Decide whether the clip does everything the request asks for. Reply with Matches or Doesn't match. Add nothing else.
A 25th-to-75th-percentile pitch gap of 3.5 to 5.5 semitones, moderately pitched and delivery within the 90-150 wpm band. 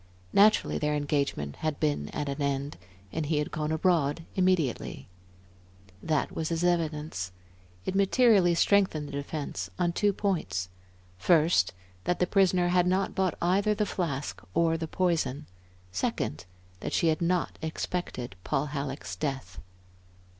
Matches